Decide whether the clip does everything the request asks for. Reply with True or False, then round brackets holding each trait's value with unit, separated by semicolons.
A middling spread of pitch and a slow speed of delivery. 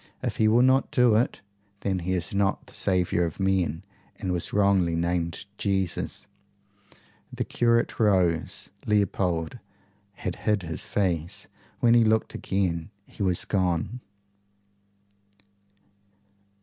True (3.4 semitones; 125 wpm)